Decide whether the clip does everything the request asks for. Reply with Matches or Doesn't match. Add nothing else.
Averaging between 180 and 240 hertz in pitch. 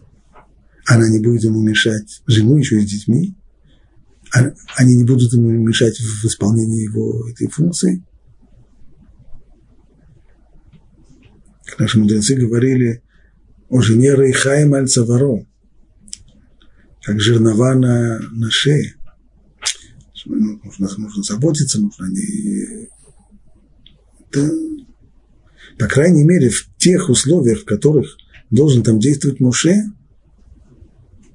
Doesn't match